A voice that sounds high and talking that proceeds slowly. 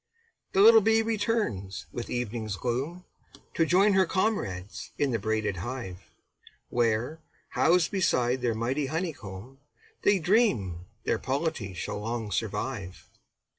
No: low, 125 Hz; slow, 125 wpm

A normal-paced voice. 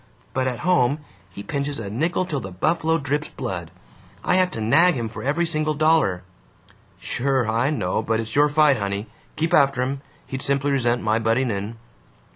Yes: average, 185 wpm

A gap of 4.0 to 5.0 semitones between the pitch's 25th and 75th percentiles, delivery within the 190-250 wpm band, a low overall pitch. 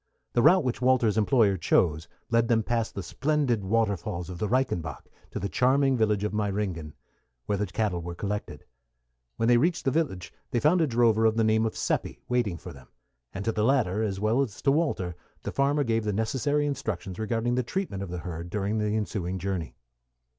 Yes: average, 4.4 semitones; average, 200 wpm; low, 110 Hz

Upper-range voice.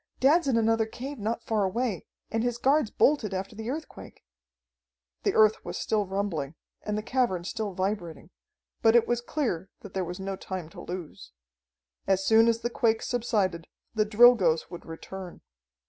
Yes: high, 215 Hz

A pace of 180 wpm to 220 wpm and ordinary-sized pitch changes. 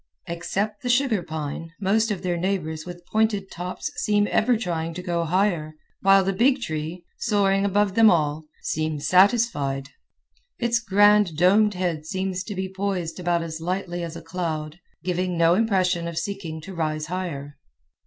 No: average, 165 wpm; average, 3.6 semitones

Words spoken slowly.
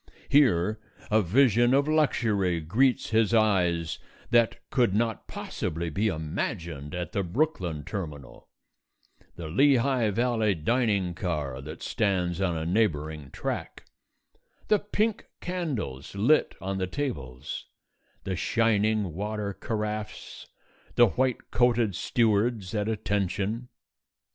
Yes: slow, 115 wpm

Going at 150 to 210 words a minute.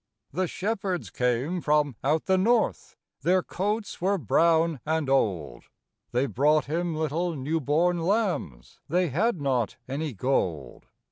No: slow, 135 wpm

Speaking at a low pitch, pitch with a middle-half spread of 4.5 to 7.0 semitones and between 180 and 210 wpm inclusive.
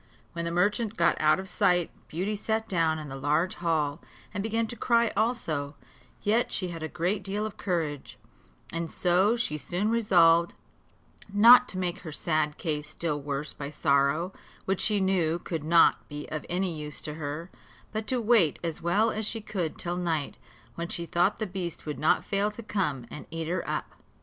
No: medium, 175 Hz; average, 4.8 semitones; average, 190 wpm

